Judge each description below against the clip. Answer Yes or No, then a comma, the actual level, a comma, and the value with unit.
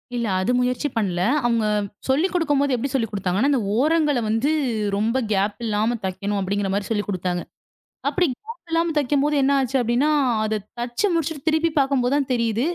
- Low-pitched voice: No, very high, 250 Hz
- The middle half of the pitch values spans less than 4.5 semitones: No, wide, 5.5 semitones